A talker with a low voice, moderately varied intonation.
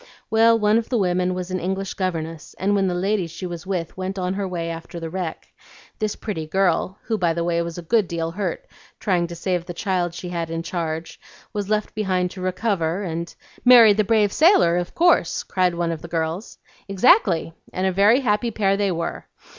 No: medium, 185 Hz; average, 3.3 semitones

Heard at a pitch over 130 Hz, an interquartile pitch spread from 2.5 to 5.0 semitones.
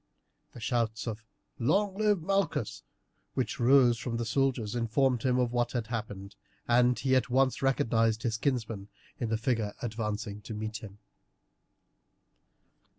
No: low, 120 Hz; average, 2.9 semitones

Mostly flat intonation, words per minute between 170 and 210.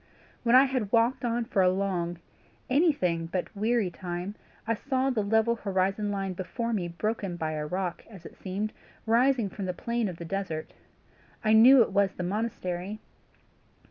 No: average, 4.2 semitones; average, 175 wpm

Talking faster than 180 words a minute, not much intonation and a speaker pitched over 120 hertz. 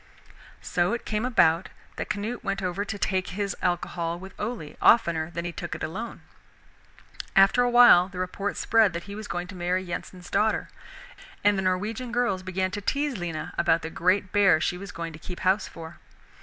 No: average, 195 wpm; average, 3.0 semitones; medium, 185 Hz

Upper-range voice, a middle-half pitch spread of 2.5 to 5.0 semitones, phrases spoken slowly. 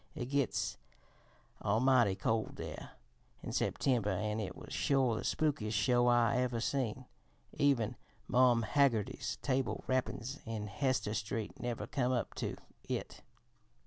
No: low, 120 Hz; average, 3.1 semitones; slow, 130 wpm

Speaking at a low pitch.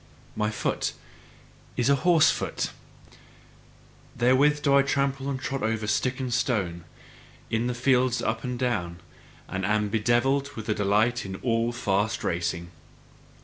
Yes: low, 120 Hz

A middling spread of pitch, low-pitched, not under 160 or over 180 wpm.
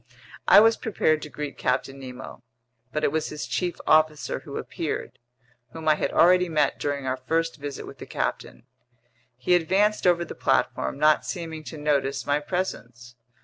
No: average, 3.8 semitones; medium, 150 Hz; average, 165 wpm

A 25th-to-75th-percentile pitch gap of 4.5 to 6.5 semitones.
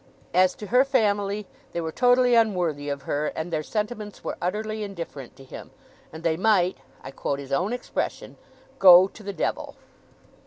Yes: average, 5.2 semitones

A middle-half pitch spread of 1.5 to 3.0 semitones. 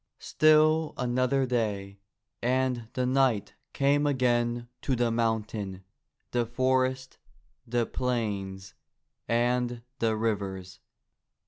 Yes: average, 2.7 semitones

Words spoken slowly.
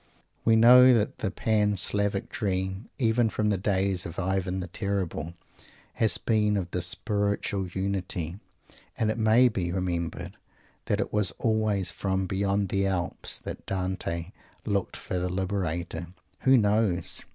No: average, 145 wpm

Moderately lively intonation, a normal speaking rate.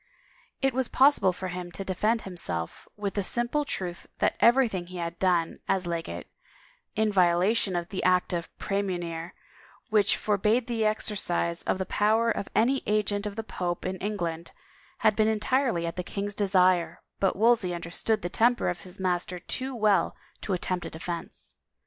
Yes: average, 3.7 semitones; average, 175 wpm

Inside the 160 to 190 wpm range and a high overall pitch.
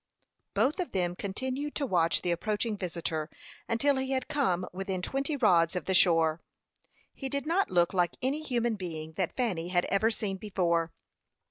Yes: average, 170 wpm; high, 195 Hz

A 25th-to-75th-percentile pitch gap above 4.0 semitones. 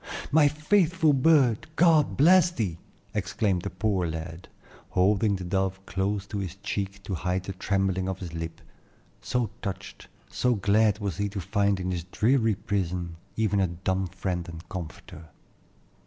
No: average, 3.4 semitones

